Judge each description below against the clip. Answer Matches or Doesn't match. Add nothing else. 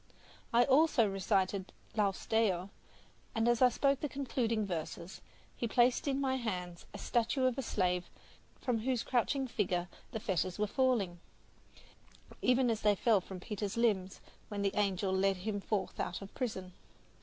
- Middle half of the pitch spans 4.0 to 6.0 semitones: Matches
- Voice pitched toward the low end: Doesn't match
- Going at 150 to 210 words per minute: Matches